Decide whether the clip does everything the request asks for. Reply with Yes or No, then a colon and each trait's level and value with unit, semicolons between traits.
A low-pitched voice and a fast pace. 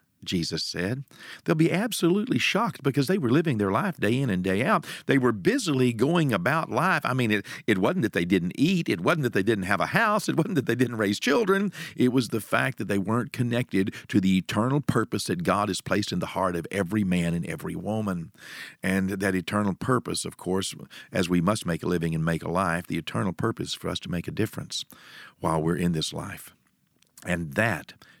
Yes: low, 110 Hz; fast, 220 wpm